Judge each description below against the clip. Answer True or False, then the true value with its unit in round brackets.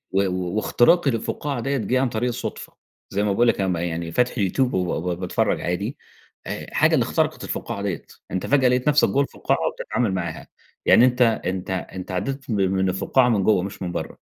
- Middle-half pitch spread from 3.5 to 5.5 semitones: True (5.2 semitones)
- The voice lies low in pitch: True (105 Hz)